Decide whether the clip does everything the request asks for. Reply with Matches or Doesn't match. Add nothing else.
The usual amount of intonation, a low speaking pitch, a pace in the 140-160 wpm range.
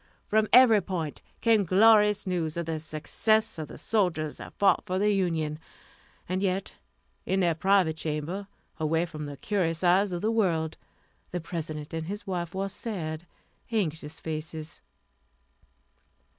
Doesn't match